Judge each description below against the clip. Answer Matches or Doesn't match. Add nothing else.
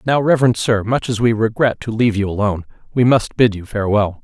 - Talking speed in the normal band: Doesn't match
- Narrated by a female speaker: Doesn't match